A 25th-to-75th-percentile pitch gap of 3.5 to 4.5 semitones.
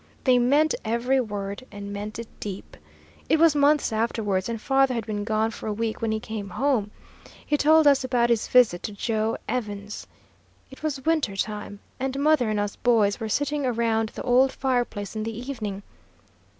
Yes: average, 4.1 semitones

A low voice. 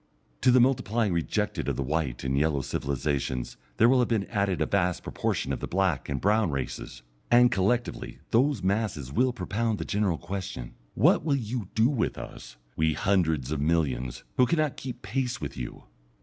Yes: very low, 95 Hz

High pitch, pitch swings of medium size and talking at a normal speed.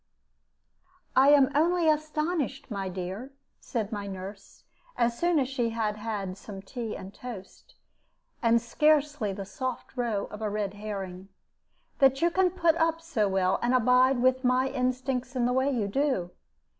Yes: high, 245 Hz; average, 5.0 semitones; average, 160 wpm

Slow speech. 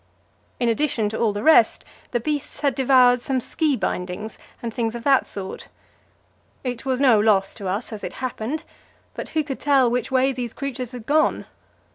No: average, 185 wpm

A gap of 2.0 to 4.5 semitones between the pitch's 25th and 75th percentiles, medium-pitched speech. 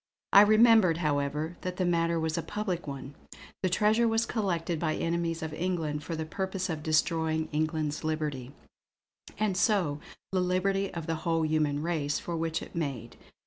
Yes: average, 2.9 semitones; medium, 165 Hz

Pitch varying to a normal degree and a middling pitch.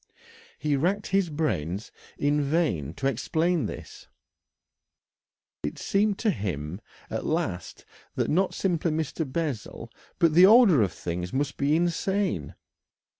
No: wide, 8.0 semitones; medium, 155 Hz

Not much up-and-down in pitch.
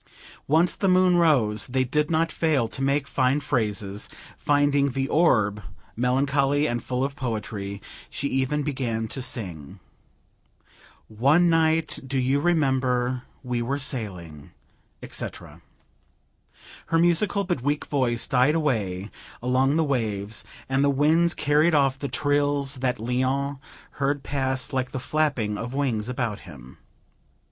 No: average, 3.6 semitones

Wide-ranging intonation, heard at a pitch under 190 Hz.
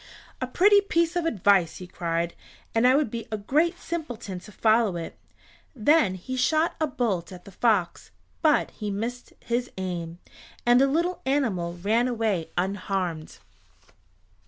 No: wide, 6.8 semitones; high, 225 Hz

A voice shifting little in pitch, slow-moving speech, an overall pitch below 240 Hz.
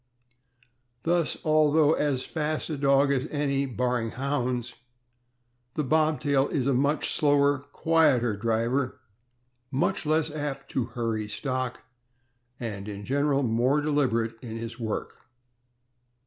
No: average, 3.6 semitones; slow, 120 wpm; low, 135 Hz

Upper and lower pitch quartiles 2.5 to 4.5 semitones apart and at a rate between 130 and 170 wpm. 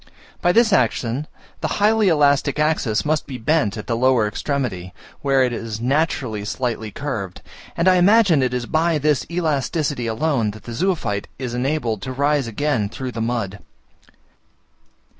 No: average, 5.2 semitones; average, 160 wpm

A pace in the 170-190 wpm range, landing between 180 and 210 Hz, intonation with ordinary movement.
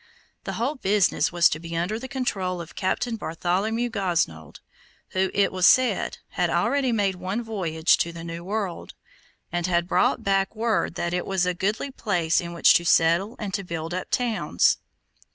Yes: average, 180 wpm; medium, 185 Hz; average, 4.1 semitones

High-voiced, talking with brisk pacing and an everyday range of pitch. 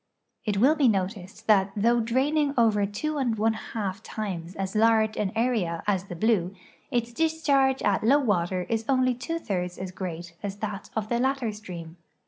No: high, 215 Hz; average, 180 wpm; average, 4.2 semitones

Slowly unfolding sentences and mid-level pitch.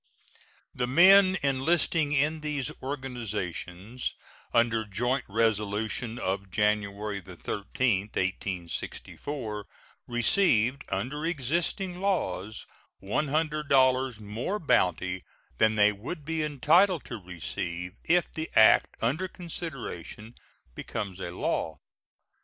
No: slow, 95 wpm; low, 120 Hz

